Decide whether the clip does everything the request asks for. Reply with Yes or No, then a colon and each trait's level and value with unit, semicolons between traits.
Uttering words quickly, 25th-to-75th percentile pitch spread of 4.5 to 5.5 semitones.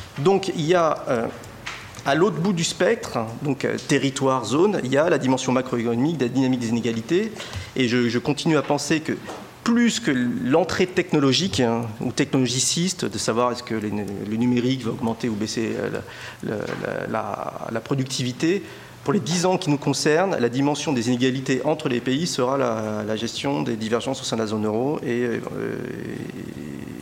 No: average, 180 wpm; average, 4.8 semitones